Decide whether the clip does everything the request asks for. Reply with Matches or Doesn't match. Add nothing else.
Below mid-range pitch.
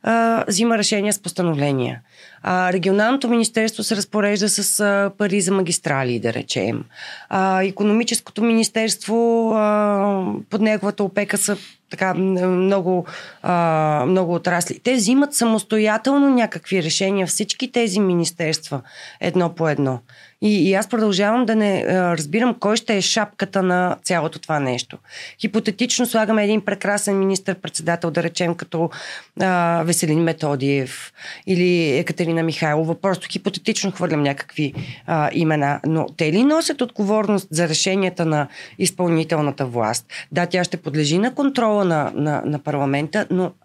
Doesn't match